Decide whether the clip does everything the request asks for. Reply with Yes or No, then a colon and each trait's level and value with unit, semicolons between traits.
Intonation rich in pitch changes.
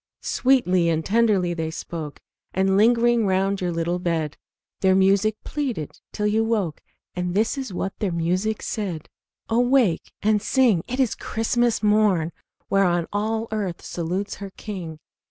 No: average, 4.1 semitones